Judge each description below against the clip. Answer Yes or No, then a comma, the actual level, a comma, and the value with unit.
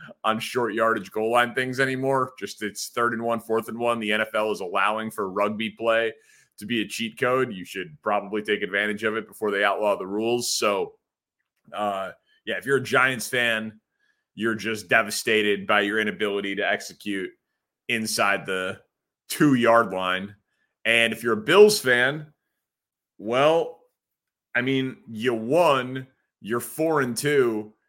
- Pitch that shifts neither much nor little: Yes, average, 3.4 semitones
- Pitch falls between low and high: No, low, 115 Hz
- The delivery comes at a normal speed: Yes, average, 160 wpm